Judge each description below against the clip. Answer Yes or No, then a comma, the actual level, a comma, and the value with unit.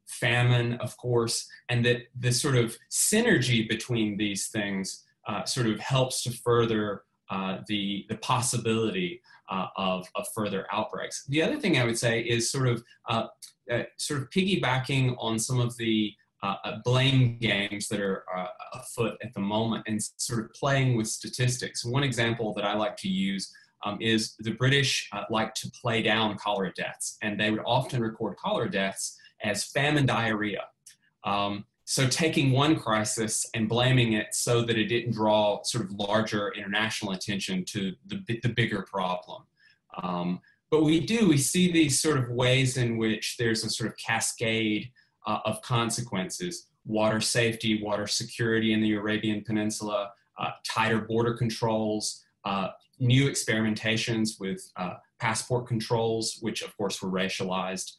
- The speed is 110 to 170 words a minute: Yes, average, 160 wpm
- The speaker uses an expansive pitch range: No, average, 2.8 semitones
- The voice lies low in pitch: Yes, low, 115 Hz